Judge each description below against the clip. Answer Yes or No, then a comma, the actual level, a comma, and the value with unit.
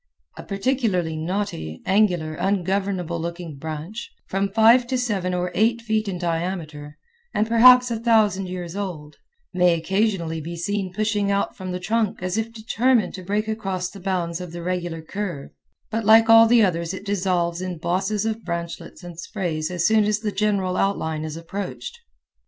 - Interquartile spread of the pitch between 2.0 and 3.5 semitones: No, average, 3.9 semitones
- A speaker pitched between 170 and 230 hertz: Yes, high, 190 Hz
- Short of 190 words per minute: Yes, average, 170 wpm